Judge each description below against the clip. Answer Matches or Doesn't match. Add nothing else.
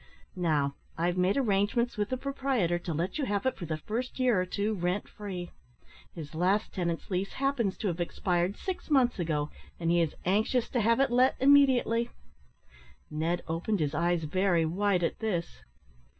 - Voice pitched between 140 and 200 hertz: Matches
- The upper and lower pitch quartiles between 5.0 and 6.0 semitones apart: Matches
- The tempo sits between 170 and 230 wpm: Matches